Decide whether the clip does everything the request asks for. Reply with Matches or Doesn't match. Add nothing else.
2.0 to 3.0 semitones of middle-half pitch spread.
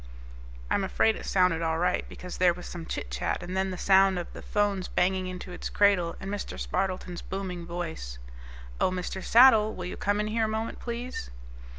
Matches